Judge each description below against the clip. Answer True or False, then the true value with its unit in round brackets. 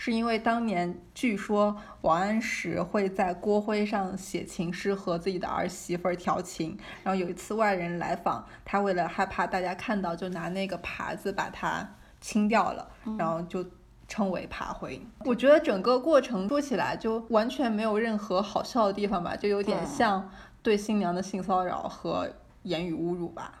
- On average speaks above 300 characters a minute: False (265 characters per minute)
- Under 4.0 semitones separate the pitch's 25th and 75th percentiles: True (3.4 semitones)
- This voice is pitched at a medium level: False (195 Hz)